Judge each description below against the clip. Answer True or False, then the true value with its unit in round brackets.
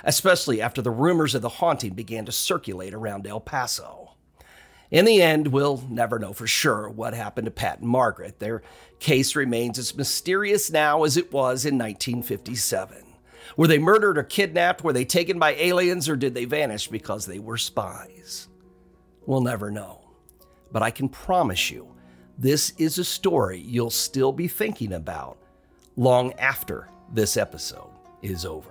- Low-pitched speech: True (125 Hz)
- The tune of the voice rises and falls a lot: True (6.0 semitones)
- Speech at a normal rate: True (165 wpm)